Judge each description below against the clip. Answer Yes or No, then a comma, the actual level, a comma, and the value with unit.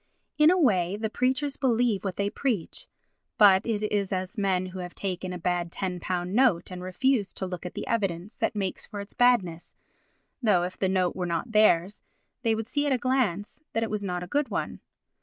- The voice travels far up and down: No, average, 4.3 semitones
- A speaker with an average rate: No, fast, 210 wpm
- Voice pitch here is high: Yes, high, 200 Hz